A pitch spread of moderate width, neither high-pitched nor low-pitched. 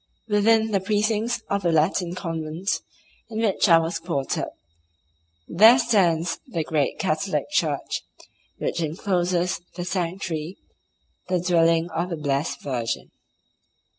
Yes: average, 3.5 semitones; medium, 175 Hz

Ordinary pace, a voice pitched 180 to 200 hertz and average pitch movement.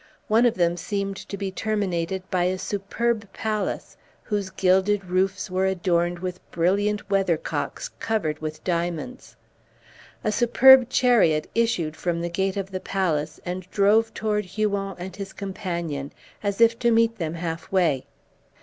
Yes: average, 150 wpm; high, 190 Hz; average, 3.3 semitones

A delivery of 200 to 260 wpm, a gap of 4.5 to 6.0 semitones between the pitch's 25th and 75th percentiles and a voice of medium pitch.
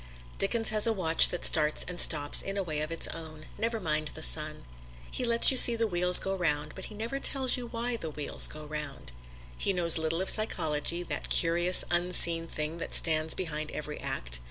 Yes: fast, 205 wpm; average, 5.1 semitones; medium, 170 Hz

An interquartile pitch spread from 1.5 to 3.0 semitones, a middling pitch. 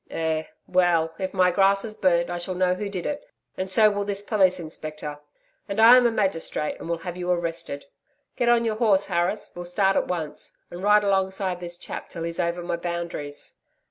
Yes: average, 2.7 semitones; medium, 180 Hz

